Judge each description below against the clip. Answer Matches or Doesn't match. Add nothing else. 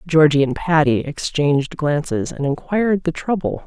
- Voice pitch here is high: Doesn't match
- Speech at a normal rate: Matches